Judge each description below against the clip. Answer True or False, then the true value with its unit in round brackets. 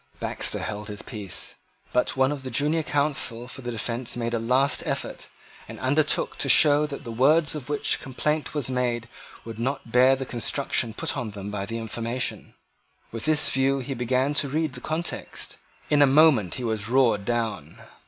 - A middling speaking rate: True (185 wpm)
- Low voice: True (125 Hz)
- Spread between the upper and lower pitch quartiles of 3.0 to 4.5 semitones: True (3.7 semitones)